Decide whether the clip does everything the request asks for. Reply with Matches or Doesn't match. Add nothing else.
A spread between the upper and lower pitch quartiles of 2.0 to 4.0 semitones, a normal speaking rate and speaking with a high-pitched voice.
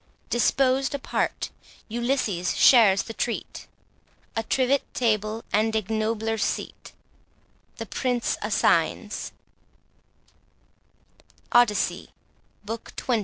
Doesn't match